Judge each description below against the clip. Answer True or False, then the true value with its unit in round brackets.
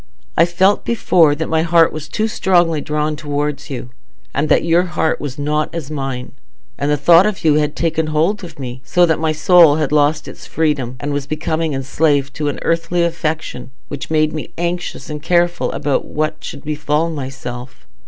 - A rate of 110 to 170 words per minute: False (190 wpm)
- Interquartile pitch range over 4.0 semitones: False (2.4 semitones)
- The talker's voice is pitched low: False (155 Hz)